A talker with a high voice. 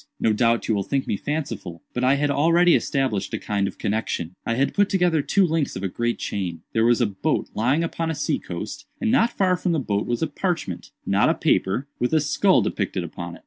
No: low, 130 Hz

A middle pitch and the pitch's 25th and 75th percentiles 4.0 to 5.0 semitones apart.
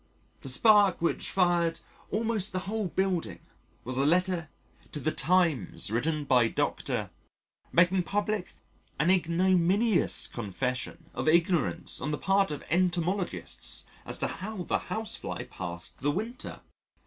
Yes: medium, 175 Hz; average, 4.3 semitones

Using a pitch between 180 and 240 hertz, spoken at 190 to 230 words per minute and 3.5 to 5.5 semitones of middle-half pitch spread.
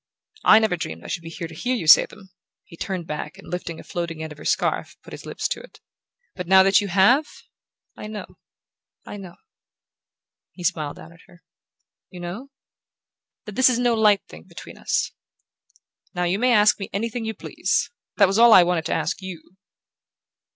Yes: high, 190 Hz; average, 200 wpm; average, 4.2 semitones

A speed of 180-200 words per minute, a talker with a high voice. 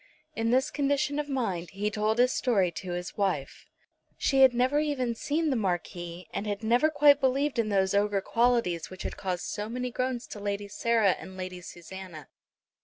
Yes: average, 185 wpm; high, 215 Hz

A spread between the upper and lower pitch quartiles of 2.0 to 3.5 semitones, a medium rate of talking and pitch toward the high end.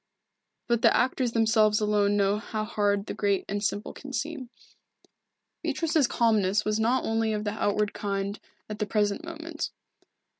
Yes: narrow, 2.5 semitones; average, 155 wpm; high, 215 Hz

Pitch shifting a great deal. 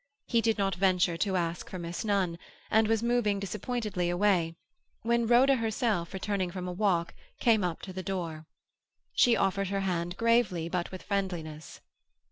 No: average, 3.8 semitones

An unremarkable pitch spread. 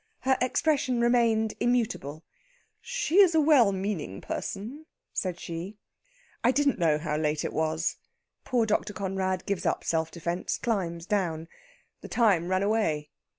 No: wide, 6.3 semitones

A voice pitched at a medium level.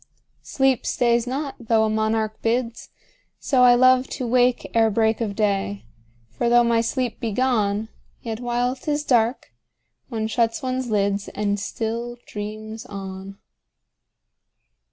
No: high, 230 Hz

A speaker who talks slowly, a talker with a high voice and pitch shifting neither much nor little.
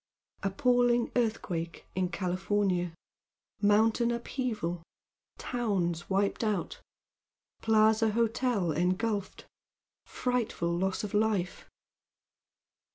Yes: slow, 75 wpm; high, 205 Hz; average, 4.2 semitones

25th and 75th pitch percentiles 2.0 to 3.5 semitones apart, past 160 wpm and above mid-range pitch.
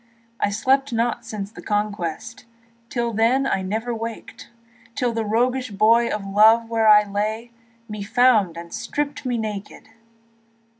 No: narrow, 2.5 semitones; average, 145 wpm; high, 225 Hz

